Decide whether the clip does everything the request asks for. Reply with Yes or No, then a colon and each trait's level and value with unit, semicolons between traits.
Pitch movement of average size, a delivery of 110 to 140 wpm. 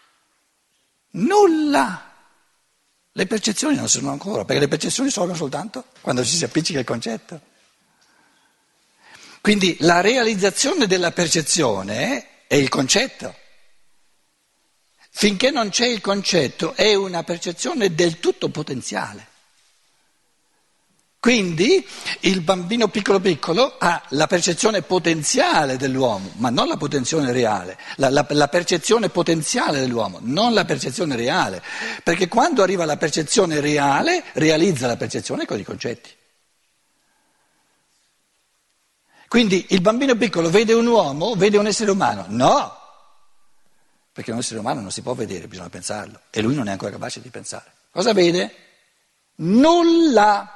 No: wide, 6.0 semitones; average, 125 wpm